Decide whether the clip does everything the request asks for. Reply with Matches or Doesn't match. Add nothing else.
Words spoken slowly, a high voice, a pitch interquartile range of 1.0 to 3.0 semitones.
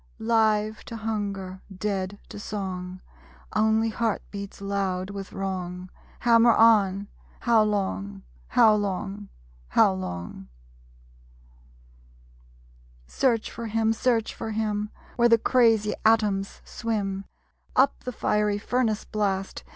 Matches